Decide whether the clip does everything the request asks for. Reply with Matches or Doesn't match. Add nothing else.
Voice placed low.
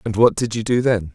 Matches